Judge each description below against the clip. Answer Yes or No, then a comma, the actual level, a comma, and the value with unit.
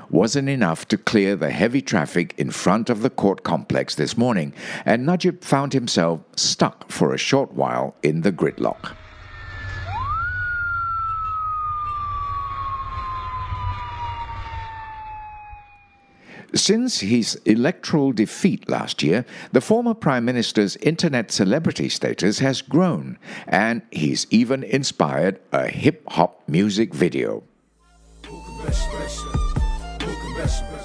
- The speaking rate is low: Yes, slow, 100 wpm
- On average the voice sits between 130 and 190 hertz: Yes, medium, 140 Hz